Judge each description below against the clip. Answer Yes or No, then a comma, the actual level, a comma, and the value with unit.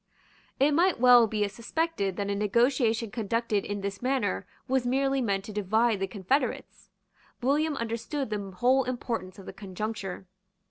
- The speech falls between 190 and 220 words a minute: No, average, 150 wpm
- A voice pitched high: Yes, high, 230 Hz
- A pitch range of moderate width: Yes, average, 4.3 semitones